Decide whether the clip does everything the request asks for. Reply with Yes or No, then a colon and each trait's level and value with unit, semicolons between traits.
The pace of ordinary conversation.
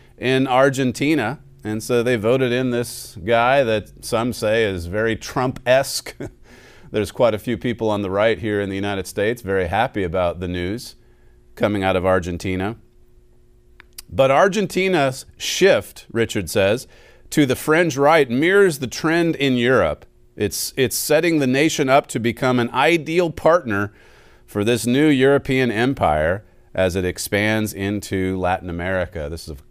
Yes: average, 155 wpm